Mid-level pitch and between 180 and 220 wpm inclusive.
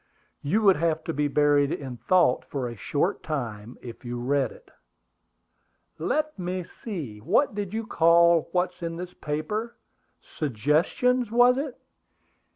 No: medium, 165 Hz; average, 145 wpm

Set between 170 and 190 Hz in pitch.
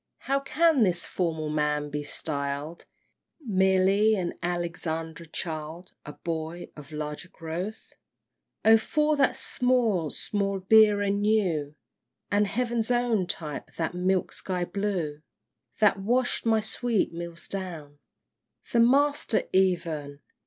Yes: medium, 185 Hz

